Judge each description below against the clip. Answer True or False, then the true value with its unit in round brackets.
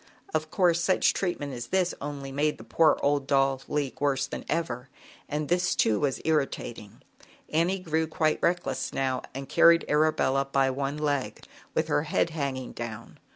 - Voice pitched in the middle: True (145 Hz)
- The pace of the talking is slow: False (165 wpm)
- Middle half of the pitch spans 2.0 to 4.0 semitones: True (2.9 semitones)